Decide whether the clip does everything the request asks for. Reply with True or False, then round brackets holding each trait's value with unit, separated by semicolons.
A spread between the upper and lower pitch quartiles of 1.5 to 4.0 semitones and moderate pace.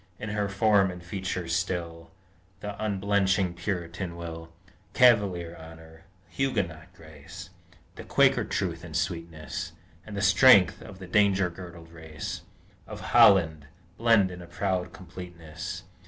False (2.9 semitones; 125 wpm)